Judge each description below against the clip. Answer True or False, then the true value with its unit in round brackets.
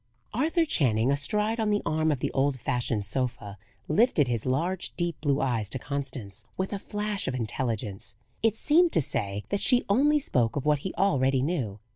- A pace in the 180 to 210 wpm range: True (185 wpm)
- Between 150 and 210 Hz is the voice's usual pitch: False (140 Hz)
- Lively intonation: True (8.8 semitones)